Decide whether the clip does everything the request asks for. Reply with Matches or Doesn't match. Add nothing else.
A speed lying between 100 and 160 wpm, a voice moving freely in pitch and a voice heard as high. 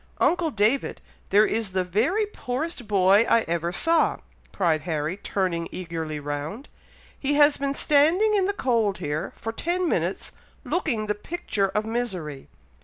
Matches